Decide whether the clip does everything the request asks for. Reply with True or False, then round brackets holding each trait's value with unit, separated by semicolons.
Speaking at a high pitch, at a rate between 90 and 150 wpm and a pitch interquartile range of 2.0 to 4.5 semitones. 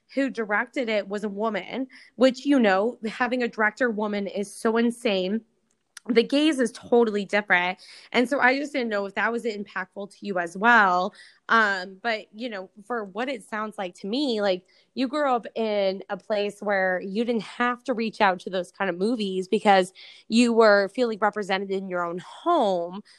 False (215 Hz; 195 wpm; 3.5 semitones)